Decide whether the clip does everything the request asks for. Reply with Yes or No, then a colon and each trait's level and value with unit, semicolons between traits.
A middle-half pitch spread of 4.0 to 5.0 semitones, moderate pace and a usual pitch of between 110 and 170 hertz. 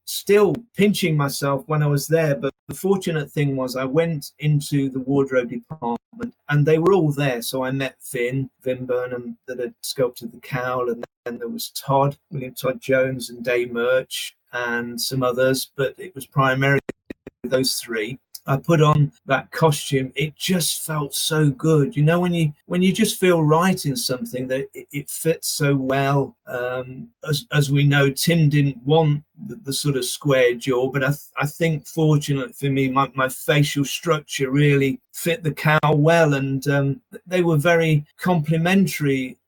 No: average, 3.3 semitones; average, 180 wpm; medium, 140 Hz